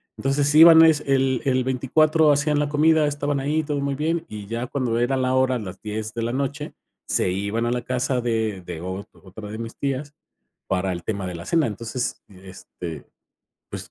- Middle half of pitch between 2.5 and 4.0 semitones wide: No, average, 5.2 semitones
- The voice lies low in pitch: Yes, low, 130 Hz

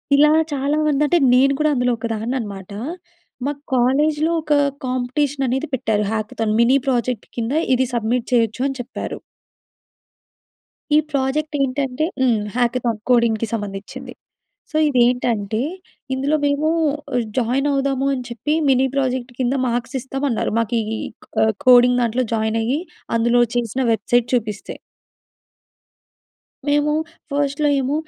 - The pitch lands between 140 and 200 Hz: No, very high, 250 Hz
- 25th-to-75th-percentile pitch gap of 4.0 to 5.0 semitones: No, average, 3.1 semitones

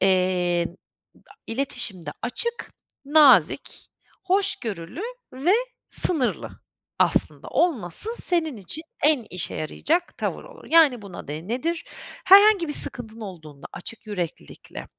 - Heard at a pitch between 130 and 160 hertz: No, high, 245 Hz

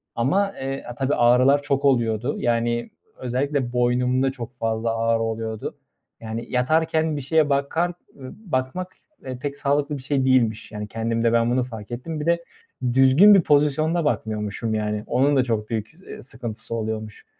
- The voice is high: No, low, 125 Hz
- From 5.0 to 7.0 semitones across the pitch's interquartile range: No, average, 3.8 semitones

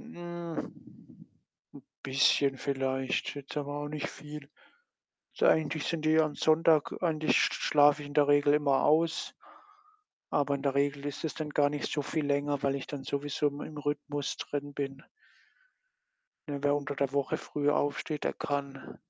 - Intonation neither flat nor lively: No, narrow, 1.2 semitones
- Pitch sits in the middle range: Yes, medium, 145 Hz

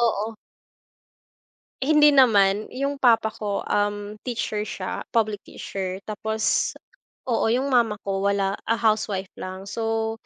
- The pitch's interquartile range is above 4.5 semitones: No, narrow, 2.5 semitones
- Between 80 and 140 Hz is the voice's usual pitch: No, high, 215 Hz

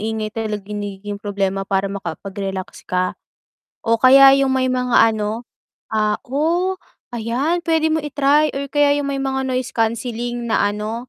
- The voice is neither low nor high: No, high, 230 Hz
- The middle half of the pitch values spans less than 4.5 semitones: No, average, 4.8 semitones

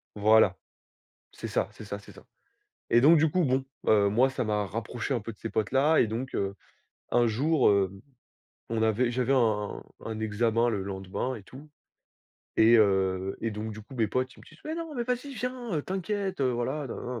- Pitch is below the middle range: Yes, low, 120 Hz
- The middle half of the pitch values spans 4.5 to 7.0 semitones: Yes, average, 4.9 semitones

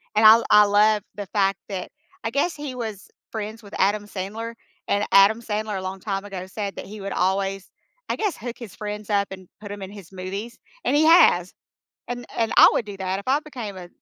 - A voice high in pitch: Yes, high, 205 Hz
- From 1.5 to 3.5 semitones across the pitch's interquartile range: Yes, narrow, 2.5 semitones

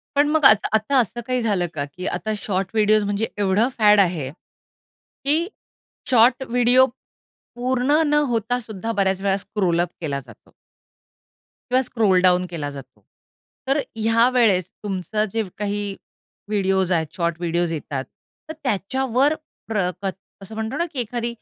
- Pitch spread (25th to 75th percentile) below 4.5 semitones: No, average, 4.8 semitones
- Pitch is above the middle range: Yes, high, 210 Hz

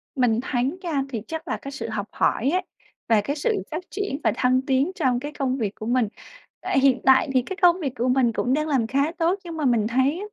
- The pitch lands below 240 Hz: No, very high, 265 Hz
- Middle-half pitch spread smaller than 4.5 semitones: Yes, average, 4.0 semitones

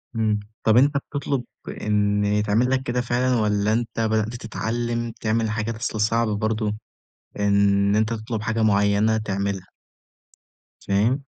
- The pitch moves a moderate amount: No, narrow, 2.1 semitones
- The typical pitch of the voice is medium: No, low, 110 Hz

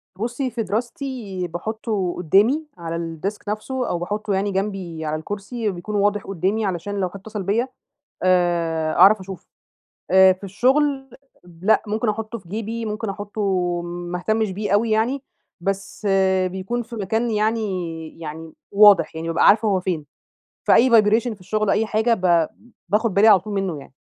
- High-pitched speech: Yes, high, 200 Hz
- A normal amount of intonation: Yes, average, 3.6 semitones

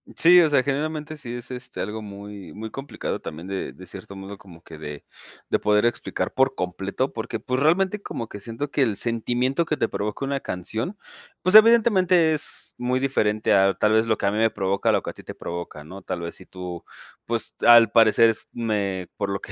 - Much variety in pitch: Yes, wide, 5.7 semitones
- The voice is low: Yes, low, 110 Hz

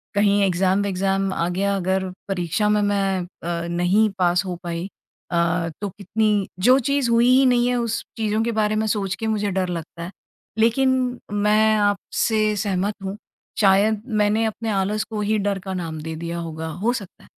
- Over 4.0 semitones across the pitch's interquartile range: No, average, 3.1 semitones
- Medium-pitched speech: No, high, 200 Hz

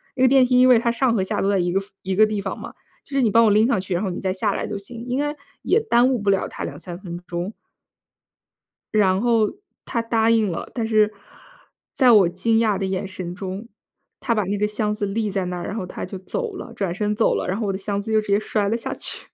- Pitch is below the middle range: No, high, 210 Hz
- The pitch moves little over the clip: No, average, 3.2 semitones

